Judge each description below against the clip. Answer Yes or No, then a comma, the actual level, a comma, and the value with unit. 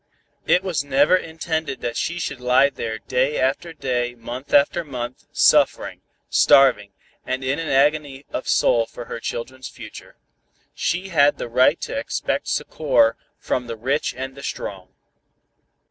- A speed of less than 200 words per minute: Yes, average, 150 wpm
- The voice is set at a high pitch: No, low, 130 Hz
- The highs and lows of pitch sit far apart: No, average, 3.5 semitones